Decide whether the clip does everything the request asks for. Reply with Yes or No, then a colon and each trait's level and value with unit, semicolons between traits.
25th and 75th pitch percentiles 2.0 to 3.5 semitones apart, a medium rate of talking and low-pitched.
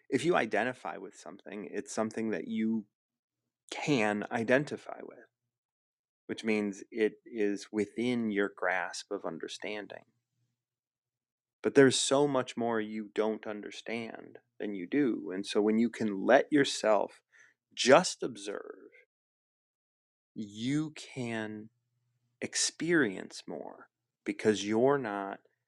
No: narrow, 2.5 semitones; slow, 110 wpm; low, 110 Hz